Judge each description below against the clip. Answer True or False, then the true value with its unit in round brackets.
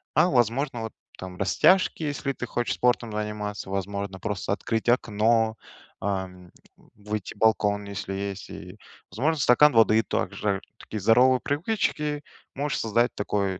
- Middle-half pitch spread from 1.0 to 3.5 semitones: False (4.0 semitones)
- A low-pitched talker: True (110 Hz)